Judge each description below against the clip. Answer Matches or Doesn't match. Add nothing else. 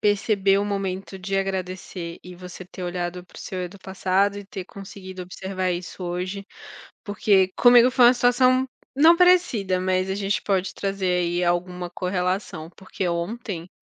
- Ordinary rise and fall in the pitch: Doesn't match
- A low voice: Doesn't match